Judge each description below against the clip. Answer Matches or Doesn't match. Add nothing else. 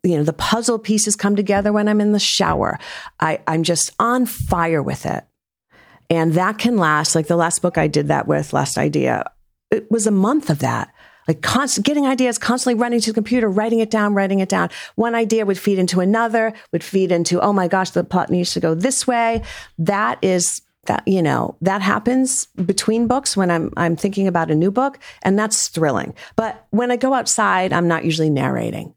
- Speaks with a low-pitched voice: Doesn't match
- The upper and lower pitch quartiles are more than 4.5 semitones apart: Matches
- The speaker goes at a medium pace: Doesn't match